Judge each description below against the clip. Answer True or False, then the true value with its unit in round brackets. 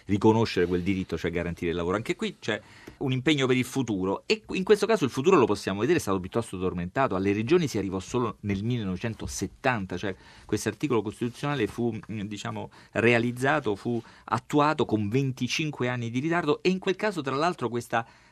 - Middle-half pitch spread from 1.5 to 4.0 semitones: False (5.1 semitones)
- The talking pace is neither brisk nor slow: False (185 wpm)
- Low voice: True (115 Hz)